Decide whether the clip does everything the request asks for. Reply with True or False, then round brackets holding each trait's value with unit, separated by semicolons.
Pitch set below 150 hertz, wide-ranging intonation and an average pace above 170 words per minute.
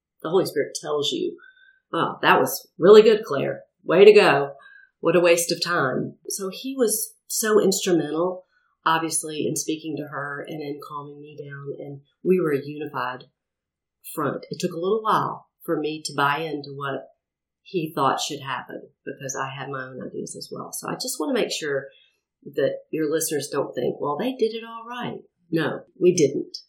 False (170 Hz; 8.7 semitones; 190 wpm)